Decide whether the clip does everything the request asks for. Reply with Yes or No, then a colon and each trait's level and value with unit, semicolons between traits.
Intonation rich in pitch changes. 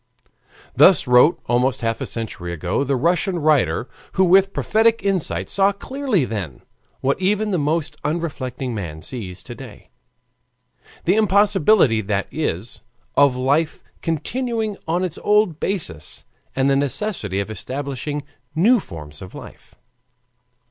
Yes: wide, 8.3 semitones